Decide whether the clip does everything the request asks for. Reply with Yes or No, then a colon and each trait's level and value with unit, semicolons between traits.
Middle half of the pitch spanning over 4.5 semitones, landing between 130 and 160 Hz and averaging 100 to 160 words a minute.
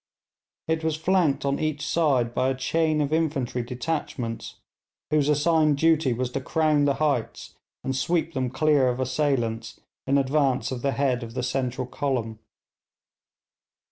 No: average, 3.4 semitones; medium, 140 Hz; average, 150 wpm